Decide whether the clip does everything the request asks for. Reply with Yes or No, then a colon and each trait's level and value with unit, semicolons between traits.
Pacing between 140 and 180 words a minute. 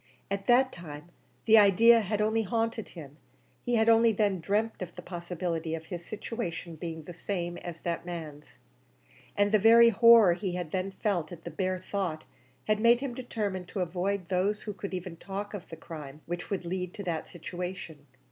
No: average, 190 wpm